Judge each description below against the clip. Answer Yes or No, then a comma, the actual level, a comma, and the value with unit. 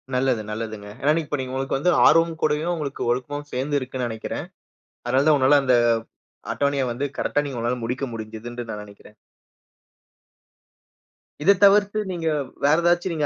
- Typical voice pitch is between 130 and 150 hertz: Yes, low, 135 Hz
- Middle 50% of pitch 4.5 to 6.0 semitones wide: No, average, 4.1 semitones